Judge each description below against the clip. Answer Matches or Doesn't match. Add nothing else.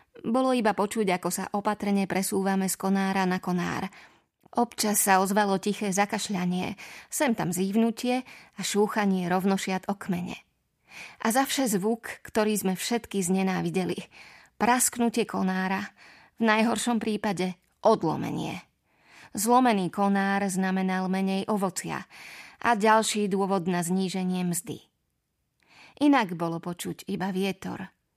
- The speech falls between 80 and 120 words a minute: Matches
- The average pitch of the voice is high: Matches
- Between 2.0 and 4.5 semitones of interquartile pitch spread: Matches